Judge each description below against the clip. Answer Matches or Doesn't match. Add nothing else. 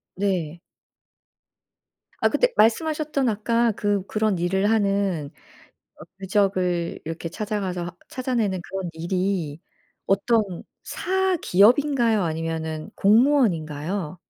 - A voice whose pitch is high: Matches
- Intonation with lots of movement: Doesn't match